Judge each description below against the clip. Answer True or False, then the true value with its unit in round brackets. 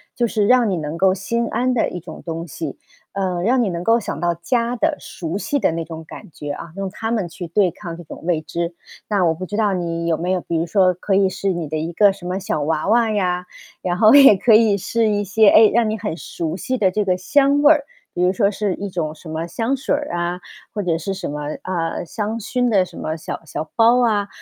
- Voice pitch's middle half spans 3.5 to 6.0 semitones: True (4.5 semitones)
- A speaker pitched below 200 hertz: True (190 Hz)